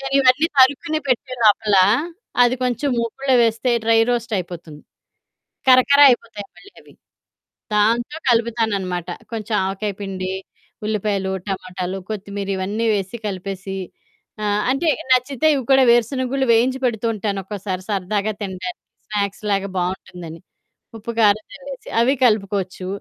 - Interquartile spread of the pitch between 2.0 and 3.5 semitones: No, average, 4.4 semitones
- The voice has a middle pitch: No, high, 215 Hz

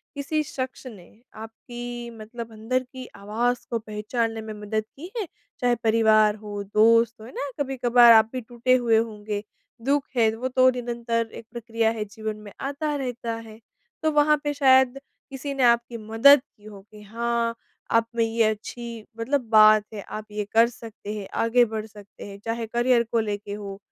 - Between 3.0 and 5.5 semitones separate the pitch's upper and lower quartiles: No, narrow, 2.5 semitones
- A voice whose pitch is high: Yes, high, 230 Hz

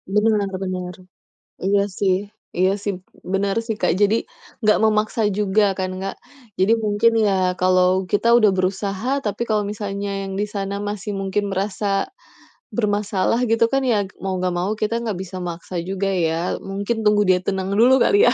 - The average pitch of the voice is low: No, high, 200 Hz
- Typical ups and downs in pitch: No, narrow, 1.9 semitones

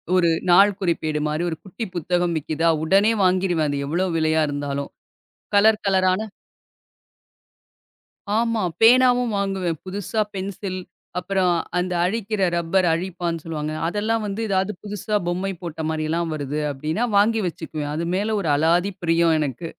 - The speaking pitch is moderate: Yes, medium, 180 Hz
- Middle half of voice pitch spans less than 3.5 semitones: No, average, 3.8 semitones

